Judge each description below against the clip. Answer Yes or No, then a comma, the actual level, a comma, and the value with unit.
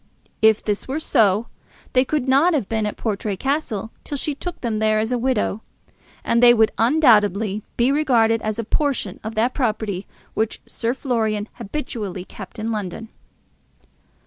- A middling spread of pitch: Yes, average, 3.4 semitones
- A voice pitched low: No, high, 225 Hz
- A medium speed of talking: Yes, average, 165 wpm